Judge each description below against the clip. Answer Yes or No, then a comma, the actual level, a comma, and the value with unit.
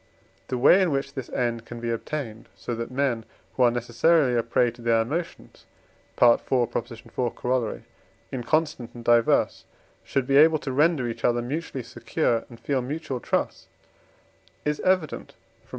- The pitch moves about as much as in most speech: Yes, average, 3.4 semitones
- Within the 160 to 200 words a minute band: Yes, average, 165 wpm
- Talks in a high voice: No, low, 125 Hz